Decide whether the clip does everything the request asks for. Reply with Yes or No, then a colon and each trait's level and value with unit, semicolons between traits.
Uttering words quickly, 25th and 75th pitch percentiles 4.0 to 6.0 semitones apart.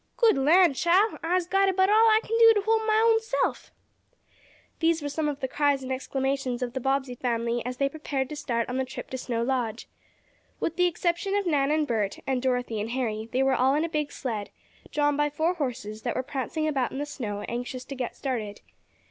Yes: fast, 215 wpm; average, 5.1 semitones